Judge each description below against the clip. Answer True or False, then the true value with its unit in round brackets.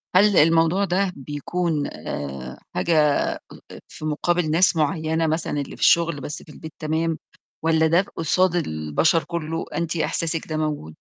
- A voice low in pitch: False (160 Hz)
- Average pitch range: False (2.1 semitones)